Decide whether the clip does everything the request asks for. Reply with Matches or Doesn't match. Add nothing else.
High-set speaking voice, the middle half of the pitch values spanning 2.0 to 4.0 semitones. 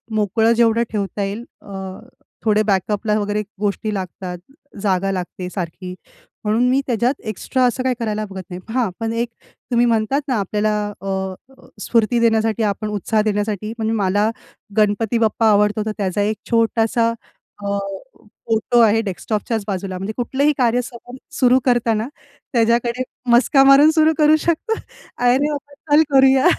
Matches